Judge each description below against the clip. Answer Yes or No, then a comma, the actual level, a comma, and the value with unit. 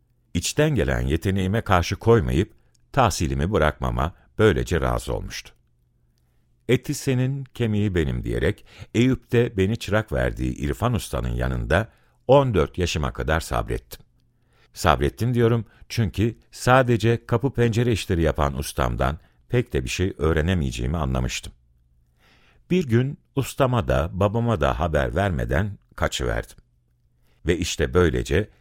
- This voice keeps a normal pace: Yes, average, 115 wpm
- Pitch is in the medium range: No, very low, 85 Hz